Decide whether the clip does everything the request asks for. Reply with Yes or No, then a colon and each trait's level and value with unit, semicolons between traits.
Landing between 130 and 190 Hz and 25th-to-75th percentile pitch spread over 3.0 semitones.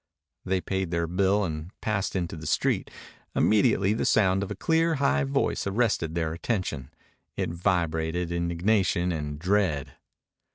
No: very low, 90 Hz; average, 3.6 semitones